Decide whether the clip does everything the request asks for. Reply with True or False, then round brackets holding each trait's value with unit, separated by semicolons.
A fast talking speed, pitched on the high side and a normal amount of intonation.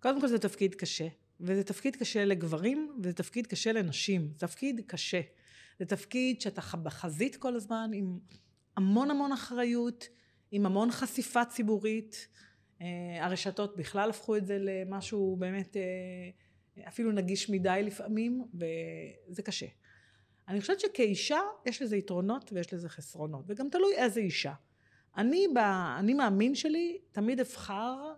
False (135 wpm; 200 Hz; 5.0 semitones)